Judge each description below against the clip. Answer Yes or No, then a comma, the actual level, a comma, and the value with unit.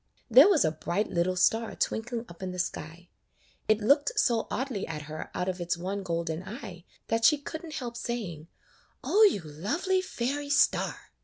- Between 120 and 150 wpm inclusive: No, average, 180 wpm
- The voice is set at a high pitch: Yes, high, 210 Hz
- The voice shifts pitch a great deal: Yes, wide, 7.1 semitones